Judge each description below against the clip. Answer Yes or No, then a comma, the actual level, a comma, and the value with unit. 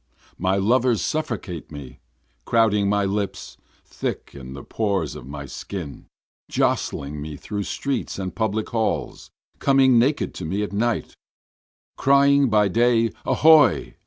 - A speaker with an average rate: No, slow, 130 wpm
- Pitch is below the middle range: Yes, low, 105 Hz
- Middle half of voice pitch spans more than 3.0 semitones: Yes, average, 5.2 semitones